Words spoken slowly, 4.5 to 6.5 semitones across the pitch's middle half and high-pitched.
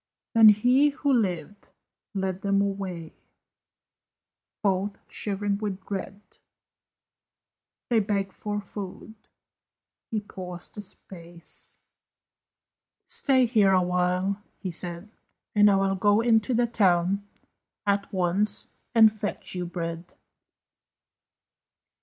No: slow, 100 wpm; narrow, 2.4 semitones; high, 200 Hz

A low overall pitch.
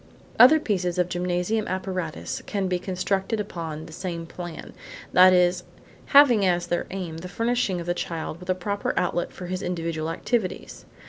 No: medium, 180 Hz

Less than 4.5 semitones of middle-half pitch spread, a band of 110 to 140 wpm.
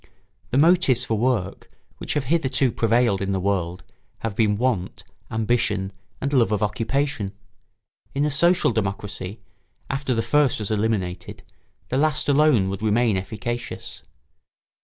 No: average, 4.9 semitones; slow, 135 wpm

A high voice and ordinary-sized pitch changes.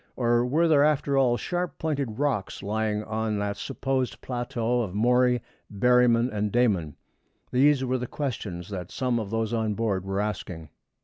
No: low, 120 Hz; average, 3.6 semitones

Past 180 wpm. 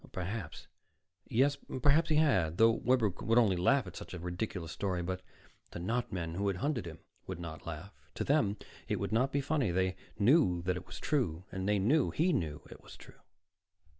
Yes: average, 200 wpm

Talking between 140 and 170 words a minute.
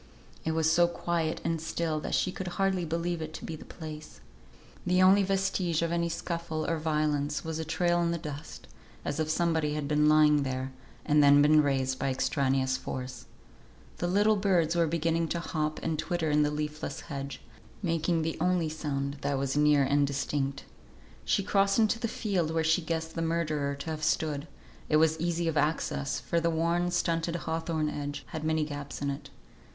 No: average, 190 wpm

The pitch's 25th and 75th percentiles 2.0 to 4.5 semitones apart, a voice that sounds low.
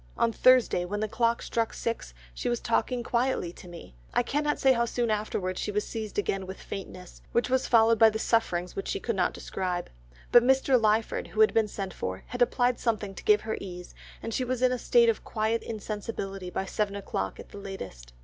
No: average, 3.5 semitones; high, 220 Hz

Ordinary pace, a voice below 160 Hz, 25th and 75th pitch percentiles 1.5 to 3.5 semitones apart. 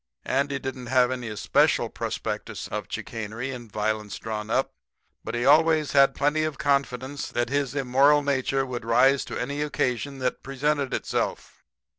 Yes: average, 155 wpm; low, 135 Hz; average, 2.7 semitones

